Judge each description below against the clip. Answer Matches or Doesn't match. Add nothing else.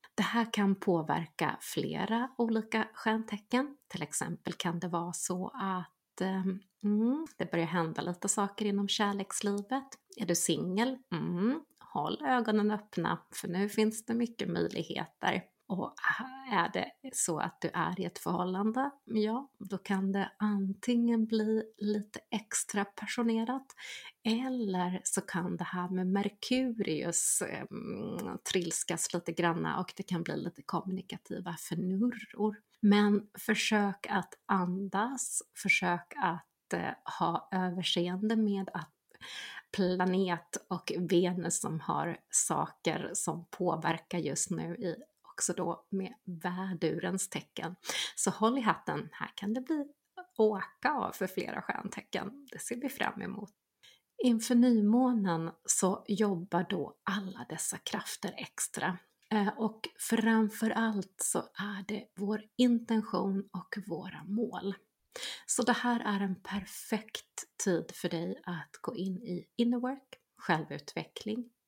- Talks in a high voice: Matches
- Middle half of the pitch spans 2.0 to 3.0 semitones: Doesn't match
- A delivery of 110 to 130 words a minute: Matches